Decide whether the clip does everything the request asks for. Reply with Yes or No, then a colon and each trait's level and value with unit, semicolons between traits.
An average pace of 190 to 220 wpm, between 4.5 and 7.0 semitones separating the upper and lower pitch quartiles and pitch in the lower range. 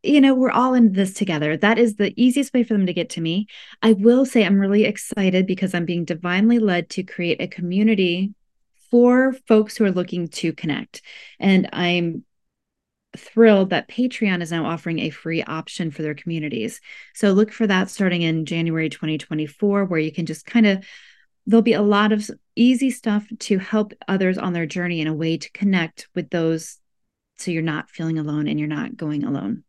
No: average, 200 wpm; average, 4.8 semitones; high, 190 Hz